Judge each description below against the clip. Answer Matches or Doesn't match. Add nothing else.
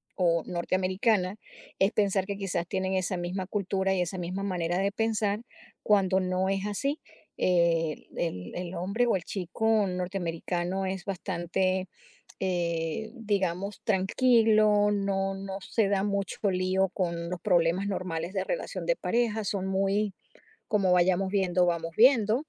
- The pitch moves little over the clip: Matches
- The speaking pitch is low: Doesn't match